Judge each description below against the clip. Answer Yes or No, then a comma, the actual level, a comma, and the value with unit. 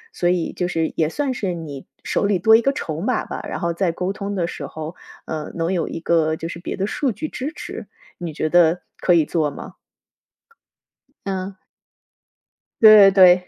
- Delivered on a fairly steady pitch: No, average, 3.3 semitones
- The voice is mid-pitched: Yes, medium, 180 Hz